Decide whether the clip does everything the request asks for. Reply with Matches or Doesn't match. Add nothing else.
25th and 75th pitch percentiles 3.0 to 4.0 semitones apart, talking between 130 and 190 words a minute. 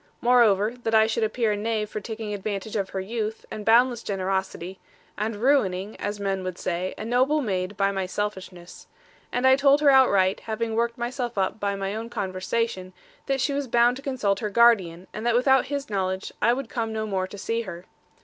Doesn't match